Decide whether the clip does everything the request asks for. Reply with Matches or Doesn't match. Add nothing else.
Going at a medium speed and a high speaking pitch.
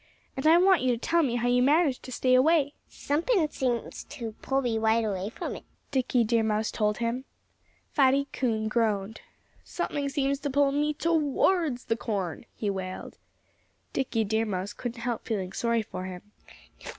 Matches